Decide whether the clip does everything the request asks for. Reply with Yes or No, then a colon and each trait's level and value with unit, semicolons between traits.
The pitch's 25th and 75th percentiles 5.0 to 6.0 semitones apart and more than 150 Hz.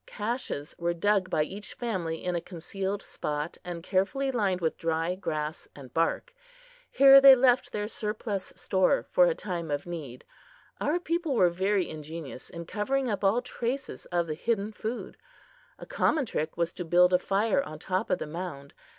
Yes: wide, 5.5 semitones; medium, 185 Hz